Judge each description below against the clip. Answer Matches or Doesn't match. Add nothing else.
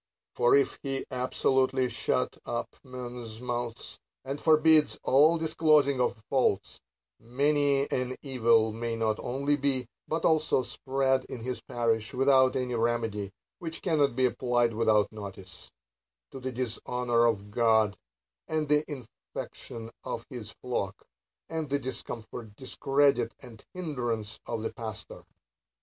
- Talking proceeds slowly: Matches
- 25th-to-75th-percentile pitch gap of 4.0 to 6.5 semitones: Doesn't match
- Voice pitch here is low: Matches